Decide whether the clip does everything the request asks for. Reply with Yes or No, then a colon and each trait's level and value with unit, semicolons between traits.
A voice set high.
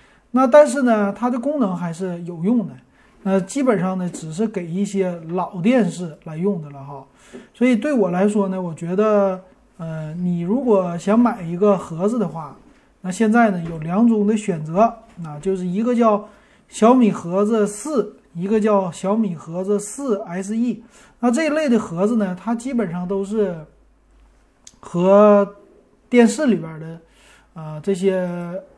Yes: high, 200 Hz